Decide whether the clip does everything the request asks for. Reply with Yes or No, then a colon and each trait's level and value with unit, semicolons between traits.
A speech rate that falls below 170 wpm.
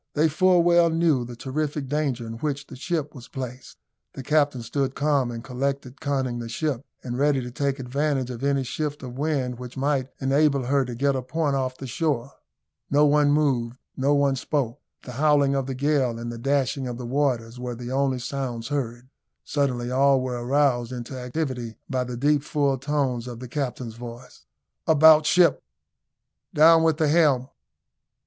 No: average, 185 wpm